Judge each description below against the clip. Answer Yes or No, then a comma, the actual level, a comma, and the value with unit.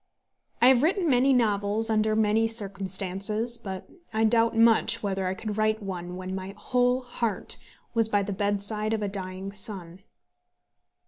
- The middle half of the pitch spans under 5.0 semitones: Yes, average, 2.8 semitones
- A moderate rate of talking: Yes, average, 155 wpm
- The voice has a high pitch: Yes, high, 215 Hz